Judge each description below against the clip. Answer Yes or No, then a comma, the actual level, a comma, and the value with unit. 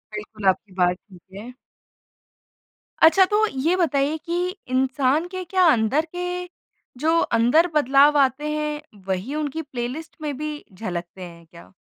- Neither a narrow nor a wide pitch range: No, wide, 6.2 semitones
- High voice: Yes, very high, 285 Hz